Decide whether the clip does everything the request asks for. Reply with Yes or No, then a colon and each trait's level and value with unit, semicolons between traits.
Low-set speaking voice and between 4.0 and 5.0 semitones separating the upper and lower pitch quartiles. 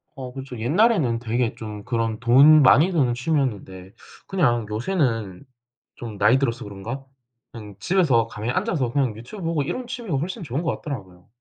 No: low, 125 Hz; wide, 5.6 semitones